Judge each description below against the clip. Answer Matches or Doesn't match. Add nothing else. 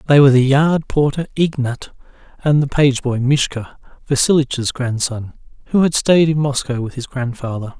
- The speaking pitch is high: Doesn't match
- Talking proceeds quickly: Doesn't match